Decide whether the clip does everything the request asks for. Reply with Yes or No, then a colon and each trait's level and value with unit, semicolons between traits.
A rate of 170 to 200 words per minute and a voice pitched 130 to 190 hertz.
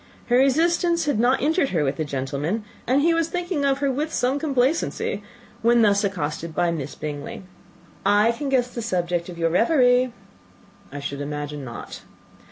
No: average, 175 wpm; high, 230 Hz